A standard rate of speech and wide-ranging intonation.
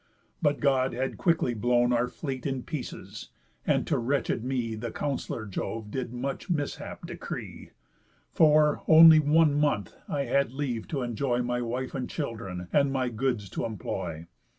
No: average, 155 wpm; average, 3.4 semitones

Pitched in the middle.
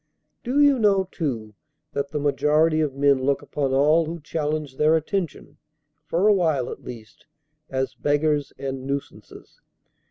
Yes: medium, 150 Hz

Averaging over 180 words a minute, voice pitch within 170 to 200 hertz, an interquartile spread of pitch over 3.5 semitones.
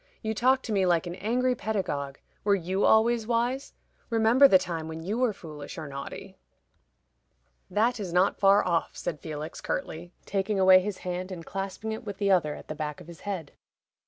Yes: average, 190 wpm; high, 190 Hz; average, 4.6 semitones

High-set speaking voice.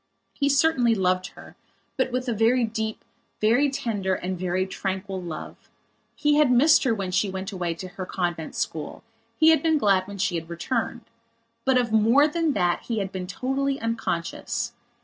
Yes: high, 220 Hz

